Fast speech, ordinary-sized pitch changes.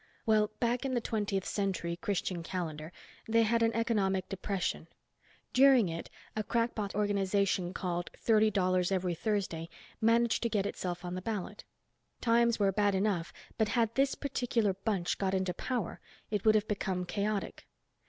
No: average, 155 wpm; average, 3.6 semitones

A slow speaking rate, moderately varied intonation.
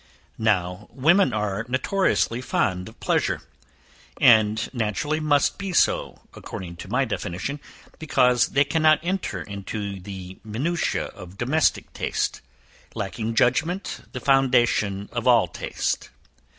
No: slow, 120 wpm; wide, 6.4 semitones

